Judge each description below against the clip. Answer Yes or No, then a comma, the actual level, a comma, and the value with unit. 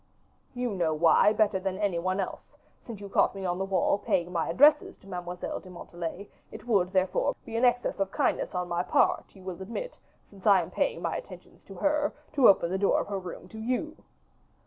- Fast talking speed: Yes, fast, 215 wpm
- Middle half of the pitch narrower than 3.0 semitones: No, average, 3.5 semitones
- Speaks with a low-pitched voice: No, high, 195 Hz